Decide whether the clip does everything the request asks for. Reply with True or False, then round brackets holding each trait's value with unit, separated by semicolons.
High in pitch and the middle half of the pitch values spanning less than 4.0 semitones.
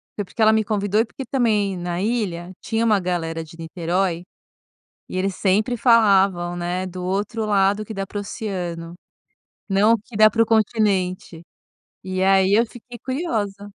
True (200 Hz; 3.2 semitones)